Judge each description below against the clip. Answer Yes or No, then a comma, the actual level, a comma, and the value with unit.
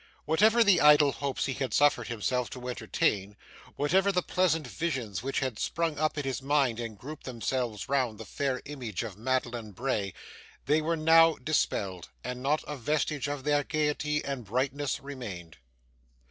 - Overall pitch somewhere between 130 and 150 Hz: Yes, low, 135 Hz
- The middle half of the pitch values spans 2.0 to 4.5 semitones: Yes, average, 4.0 semitones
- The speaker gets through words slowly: No, average, 165 wpm